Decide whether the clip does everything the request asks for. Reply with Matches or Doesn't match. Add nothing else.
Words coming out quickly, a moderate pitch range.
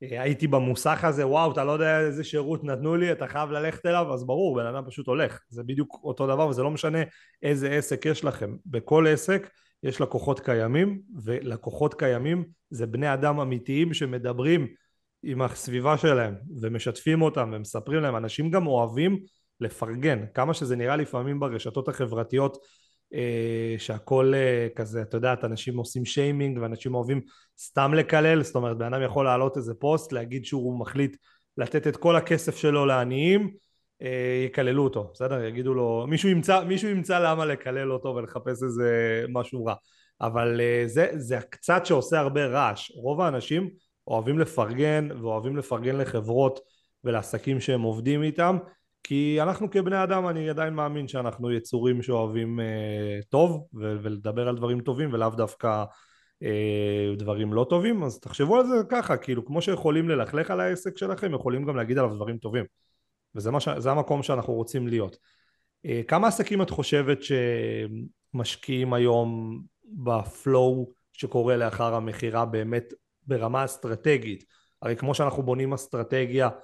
Matches